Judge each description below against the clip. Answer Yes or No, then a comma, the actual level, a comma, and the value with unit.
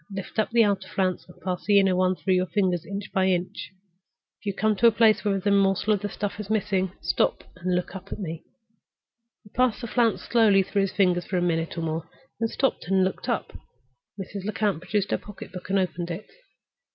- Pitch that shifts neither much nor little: No, narrow, 2.3 semitones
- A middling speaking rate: No, fast, 225 wpm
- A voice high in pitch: Yes, high, 195 Hz